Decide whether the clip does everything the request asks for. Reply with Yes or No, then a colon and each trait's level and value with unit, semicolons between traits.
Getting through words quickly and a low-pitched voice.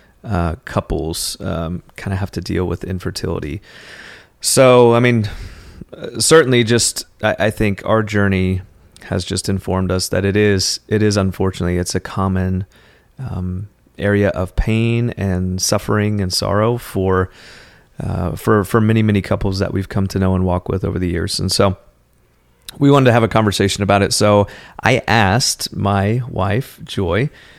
No: average, 165 wpm; low, 100 Hz